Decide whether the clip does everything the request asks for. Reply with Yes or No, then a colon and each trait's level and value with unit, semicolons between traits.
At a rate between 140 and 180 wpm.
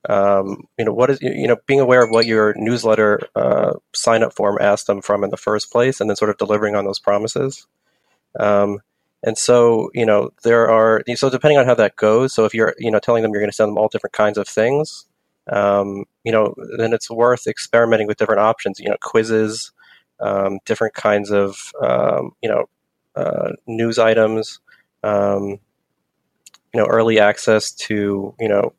No: average, 195 wpm